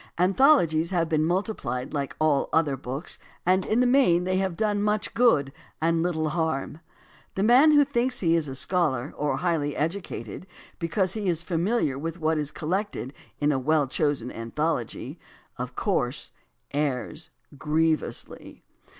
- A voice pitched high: No, medium, 165 Hz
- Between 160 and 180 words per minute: No, average, 150 wpm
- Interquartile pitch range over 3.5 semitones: Yes, average, 4.5 semitones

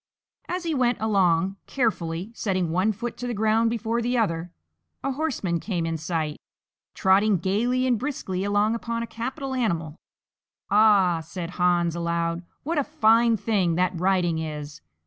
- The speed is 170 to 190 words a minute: No, average, 155 wpm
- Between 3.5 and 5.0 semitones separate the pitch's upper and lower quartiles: No, wide, 5.4 semitones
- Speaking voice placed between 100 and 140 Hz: No, high, 200 Hz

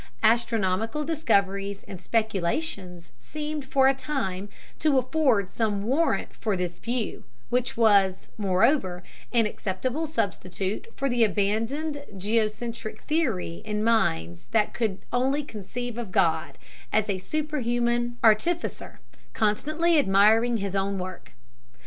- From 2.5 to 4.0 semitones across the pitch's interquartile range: No, average, 5.1 semitones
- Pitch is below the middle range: No, high, 220 Hz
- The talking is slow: Yes, slow, 120 wpm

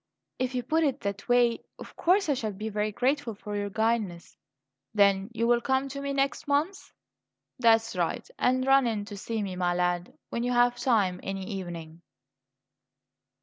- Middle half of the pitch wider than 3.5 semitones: Yes, average, 4.5 semitones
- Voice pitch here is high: Yes, high, 225 Hz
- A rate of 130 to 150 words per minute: No, average, 180 wpm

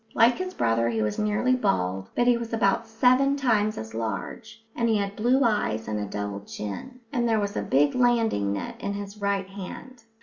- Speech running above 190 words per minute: Yes, fast, 205 wpm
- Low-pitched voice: No, high, 210 Hz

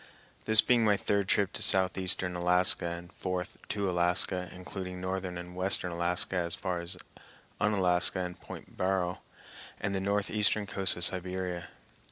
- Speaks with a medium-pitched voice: No, very low, 90 Hz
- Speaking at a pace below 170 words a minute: Yes, average, 150 wpm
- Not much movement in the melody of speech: Yes, narrow, 1.5 semitones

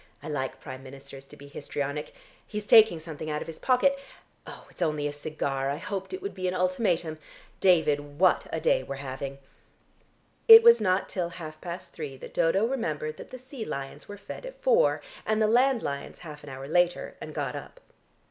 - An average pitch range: No, wide, 6.9 semitones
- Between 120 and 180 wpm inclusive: No, average, 195 wpm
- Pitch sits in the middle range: Yes, medium, 165 Hz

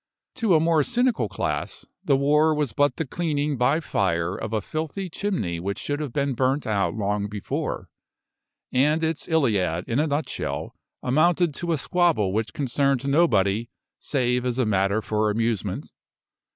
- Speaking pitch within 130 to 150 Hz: Yes, low, 135 Hz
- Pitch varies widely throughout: Yes, wide, 6.6 semitones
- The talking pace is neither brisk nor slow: Yes, average, 160 wpm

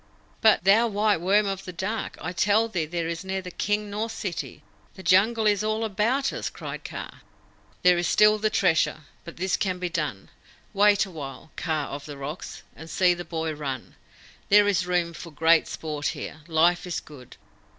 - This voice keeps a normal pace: Yes, average, 185 wpm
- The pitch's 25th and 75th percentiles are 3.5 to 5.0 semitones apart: Yes, average, 4.3 semitones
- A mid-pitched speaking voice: Yes, medium, 180 Hz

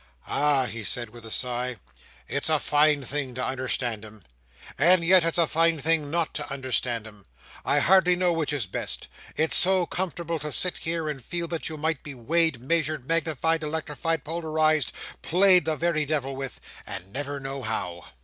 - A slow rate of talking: No, average, 180 wpm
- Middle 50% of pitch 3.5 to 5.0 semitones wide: Yes, average, 4.1 semitones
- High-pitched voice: No, medium, 150 Hz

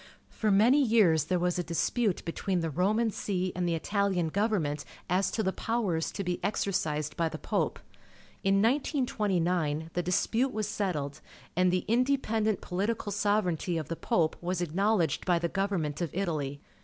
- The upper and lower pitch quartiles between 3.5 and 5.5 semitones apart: Yes, average, 4.1 semitones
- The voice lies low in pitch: No, medium, 185 Hz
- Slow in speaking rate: No, average, 165 wpm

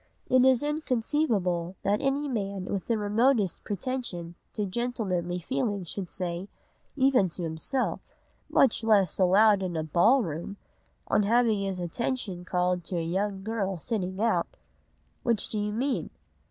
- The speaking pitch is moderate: No, high, 205 Hz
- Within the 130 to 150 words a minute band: Yes, average, 145 wpm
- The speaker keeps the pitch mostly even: No, average, 4.7 semitones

